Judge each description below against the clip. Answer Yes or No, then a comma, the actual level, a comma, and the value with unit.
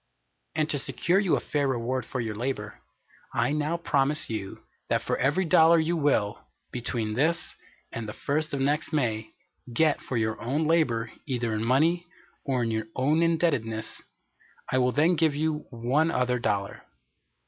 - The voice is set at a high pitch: No, low, 135 Hz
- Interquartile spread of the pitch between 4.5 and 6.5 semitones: Yes, average, 5.2 semitones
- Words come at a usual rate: Yes, average, 170 wpm